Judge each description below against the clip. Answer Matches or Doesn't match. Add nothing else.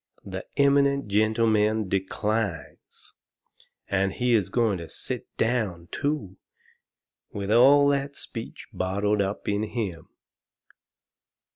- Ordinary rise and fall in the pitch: Matches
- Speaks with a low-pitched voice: Matches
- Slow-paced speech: Matches